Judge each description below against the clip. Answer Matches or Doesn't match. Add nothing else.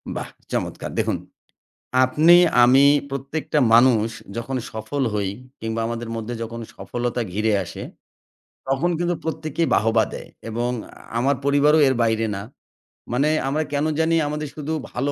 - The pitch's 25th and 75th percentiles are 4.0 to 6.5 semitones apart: Matches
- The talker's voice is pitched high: Doesn't match